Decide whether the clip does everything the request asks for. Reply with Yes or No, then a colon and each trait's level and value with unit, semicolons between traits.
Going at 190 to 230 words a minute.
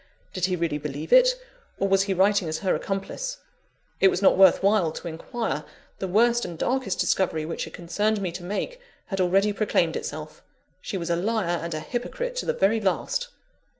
Yes: average, 195 wpm